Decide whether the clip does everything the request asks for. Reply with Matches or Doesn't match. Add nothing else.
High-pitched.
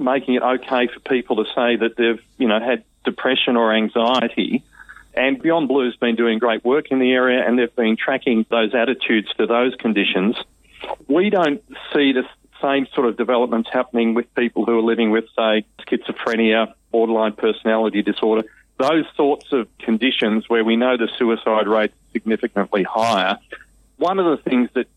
Doesn't match